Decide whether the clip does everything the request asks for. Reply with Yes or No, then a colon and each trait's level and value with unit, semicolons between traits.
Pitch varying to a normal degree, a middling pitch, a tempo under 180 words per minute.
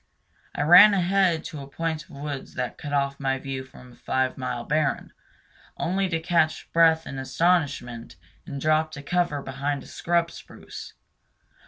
Yes: average, 3.7 semitones; medium, 150 Hz; average, 165 wpm